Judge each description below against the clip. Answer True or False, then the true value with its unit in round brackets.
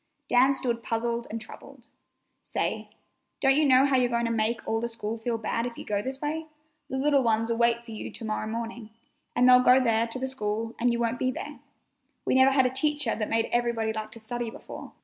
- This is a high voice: True (235 Hz)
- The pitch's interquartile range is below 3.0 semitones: True (2.4 semitones)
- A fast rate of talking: True (225 wpm)